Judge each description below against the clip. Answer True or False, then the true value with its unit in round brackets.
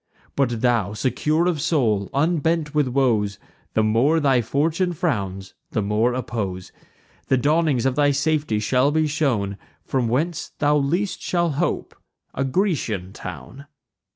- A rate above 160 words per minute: False (140 wpm)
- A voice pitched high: False (135 Hz)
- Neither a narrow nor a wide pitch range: False (5.7 semitones)